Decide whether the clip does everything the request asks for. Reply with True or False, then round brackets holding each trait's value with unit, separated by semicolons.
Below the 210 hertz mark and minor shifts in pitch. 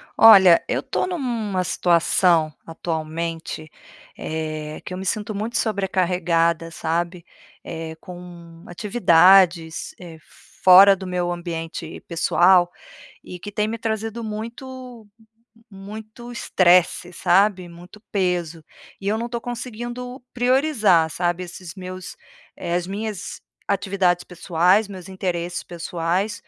False (185 Hz; 3.9 semitones)